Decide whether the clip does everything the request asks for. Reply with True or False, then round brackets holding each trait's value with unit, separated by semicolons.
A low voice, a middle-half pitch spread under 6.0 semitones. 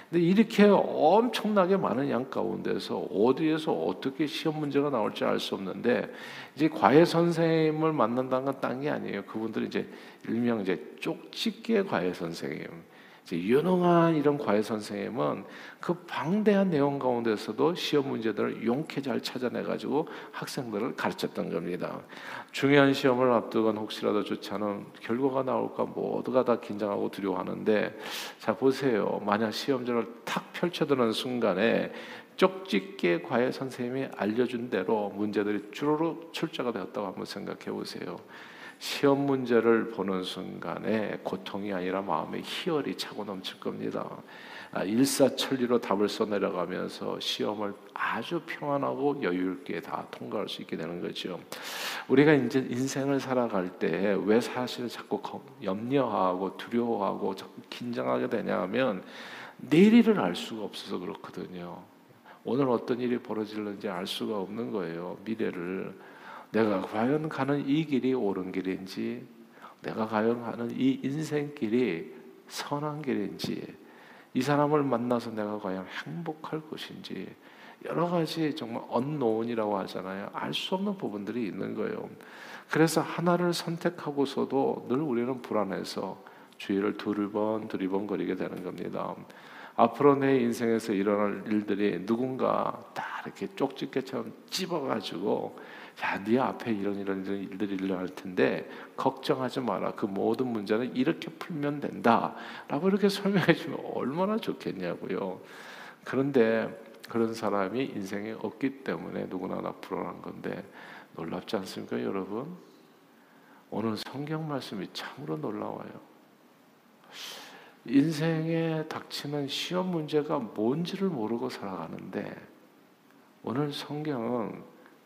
False (125 Hz; 6.4 semitones)